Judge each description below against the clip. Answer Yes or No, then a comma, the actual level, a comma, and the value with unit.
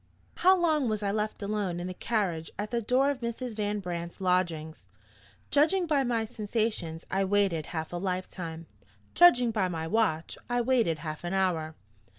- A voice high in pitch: Yes, high, 205 Hz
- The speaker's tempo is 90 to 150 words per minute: No, average, 175 wpm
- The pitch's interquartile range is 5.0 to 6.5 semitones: Yes, wide, 5.4 semitones